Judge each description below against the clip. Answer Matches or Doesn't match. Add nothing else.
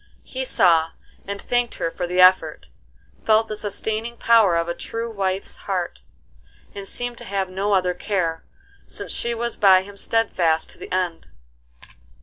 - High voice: Matches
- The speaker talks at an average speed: Matches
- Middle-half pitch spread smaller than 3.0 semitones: Doesn't match